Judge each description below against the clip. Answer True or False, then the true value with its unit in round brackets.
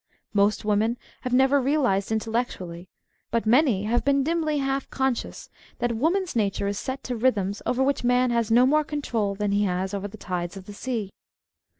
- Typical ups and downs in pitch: True (4.6 semitones)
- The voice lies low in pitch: False (235 Hz)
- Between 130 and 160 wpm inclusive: False (185 wpm)